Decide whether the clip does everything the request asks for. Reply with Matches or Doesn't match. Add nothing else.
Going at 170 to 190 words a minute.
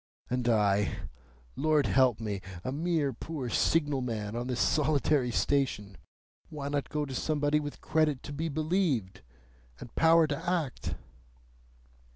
Doesn't match